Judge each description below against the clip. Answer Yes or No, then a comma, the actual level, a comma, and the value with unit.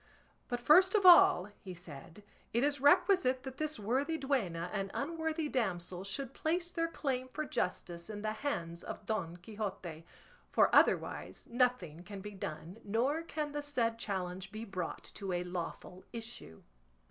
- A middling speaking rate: Yes, average, 160 wpm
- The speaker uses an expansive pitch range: Yes, wide, 7.9 semitones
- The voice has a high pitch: Yes, high, 220 Hz